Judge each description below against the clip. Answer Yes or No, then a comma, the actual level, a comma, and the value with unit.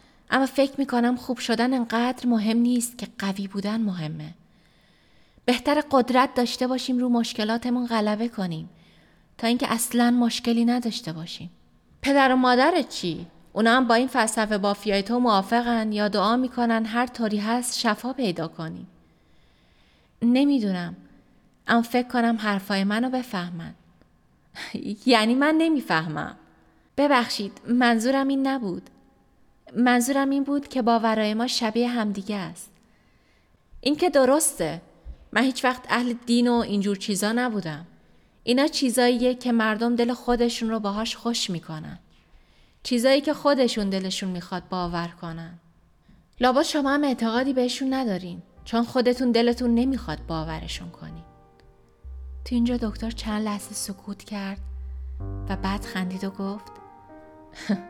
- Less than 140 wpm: Yes, average, 130 wpm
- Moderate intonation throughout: Yes, average, 4.1 semitones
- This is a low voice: No, high, 230 Hz